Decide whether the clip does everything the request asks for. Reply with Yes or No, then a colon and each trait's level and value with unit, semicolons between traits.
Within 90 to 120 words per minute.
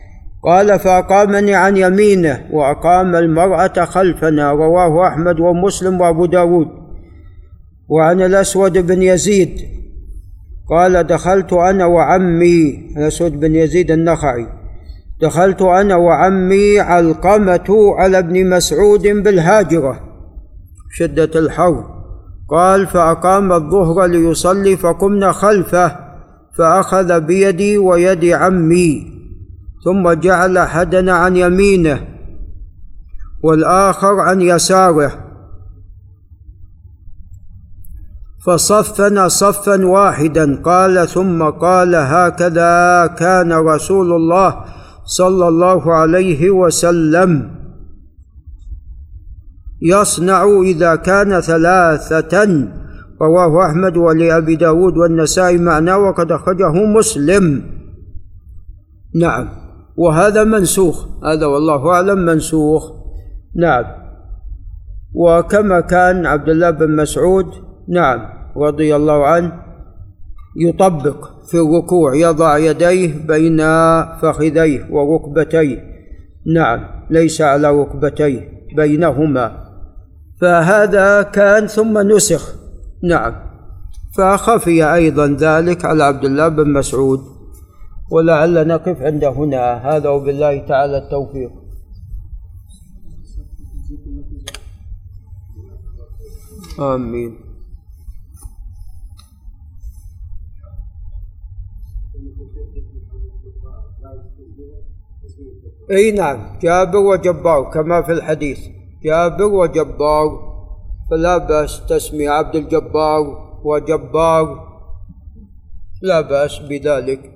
No: average, 75 wpm